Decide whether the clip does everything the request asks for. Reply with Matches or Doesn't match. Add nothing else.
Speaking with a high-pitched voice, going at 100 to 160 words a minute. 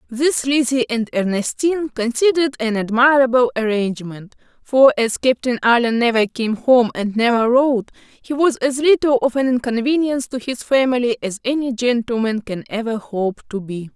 Matches